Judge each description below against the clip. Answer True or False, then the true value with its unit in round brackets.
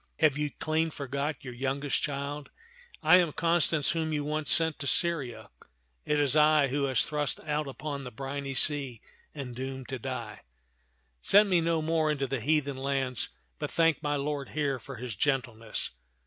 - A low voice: False (145 Hz)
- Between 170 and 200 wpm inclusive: True (175 wpm)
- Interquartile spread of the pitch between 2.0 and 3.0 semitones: True (2.5 semitones)